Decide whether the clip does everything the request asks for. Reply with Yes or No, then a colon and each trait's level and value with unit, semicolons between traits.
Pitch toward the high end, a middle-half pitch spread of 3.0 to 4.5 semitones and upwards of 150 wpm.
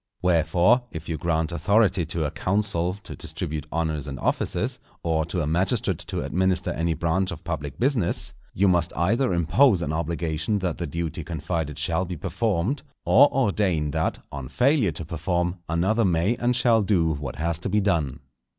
No: very low, 85 Hz; average, 3.7 semitones; average, 175 wpm